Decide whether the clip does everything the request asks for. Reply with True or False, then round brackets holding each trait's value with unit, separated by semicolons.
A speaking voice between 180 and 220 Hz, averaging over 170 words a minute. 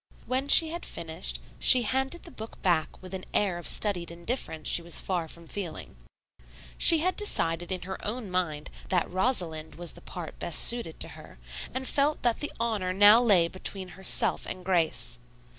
True (190 Hz; 180 wpm)